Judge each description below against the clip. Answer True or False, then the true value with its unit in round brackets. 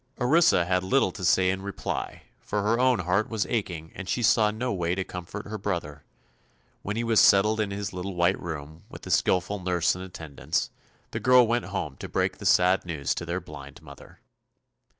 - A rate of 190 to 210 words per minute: True (200 wpm)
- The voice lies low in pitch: True (95 Hz)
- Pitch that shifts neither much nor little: True (3.6 semitones)